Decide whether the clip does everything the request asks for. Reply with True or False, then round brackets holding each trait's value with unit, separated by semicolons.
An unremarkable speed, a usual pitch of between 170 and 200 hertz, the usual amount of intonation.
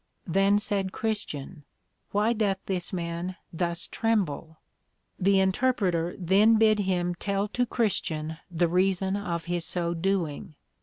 False (130 wpm; 185 Hz; 3.1 semitones)